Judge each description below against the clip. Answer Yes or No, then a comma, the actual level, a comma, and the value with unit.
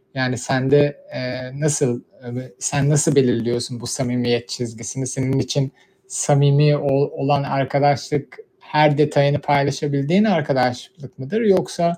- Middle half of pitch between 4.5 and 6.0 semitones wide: No, narrow, 2.4 semitones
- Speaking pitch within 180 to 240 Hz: No, medium, 140 Hz